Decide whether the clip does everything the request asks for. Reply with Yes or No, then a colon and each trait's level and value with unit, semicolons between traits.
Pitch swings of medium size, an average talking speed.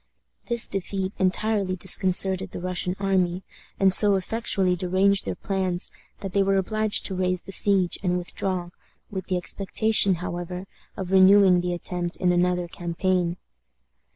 No: narrow, 1.5 semitones; average, 145 wpm